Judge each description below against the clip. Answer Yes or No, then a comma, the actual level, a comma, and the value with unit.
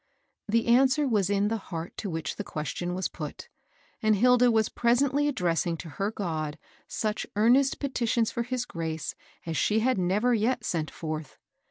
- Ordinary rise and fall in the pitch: No, wide, 6.2 semitones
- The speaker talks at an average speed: Yes, average, 175 wpm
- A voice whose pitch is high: Yes, high, 215 Hz